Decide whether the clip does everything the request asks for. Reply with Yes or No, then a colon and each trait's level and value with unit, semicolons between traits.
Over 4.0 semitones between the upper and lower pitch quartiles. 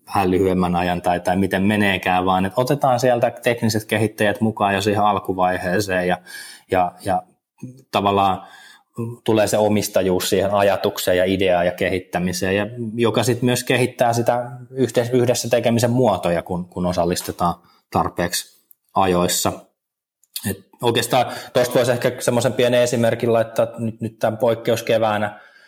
Yes: average, 4.5 semitones